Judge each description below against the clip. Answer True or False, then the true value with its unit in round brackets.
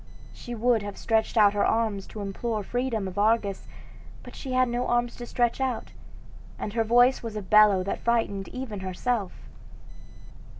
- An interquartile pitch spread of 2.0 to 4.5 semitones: True (3.0 semitones)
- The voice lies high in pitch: True (225 Hz)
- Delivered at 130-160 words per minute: False (170 wpm)